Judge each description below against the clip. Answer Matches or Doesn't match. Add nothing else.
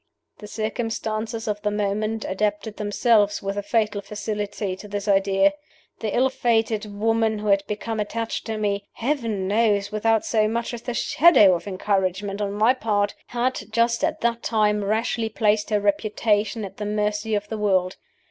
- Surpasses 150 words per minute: Matches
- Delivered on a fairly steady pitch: Matches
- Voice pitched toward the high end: Matches